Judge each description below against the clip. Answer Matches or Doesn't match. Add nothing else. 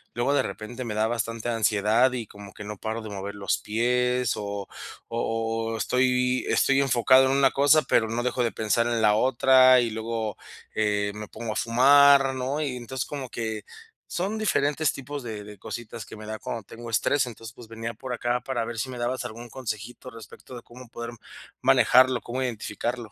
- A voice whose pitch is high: Doesn't match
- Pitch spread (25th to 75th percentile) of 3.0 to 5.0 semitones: Doesn't match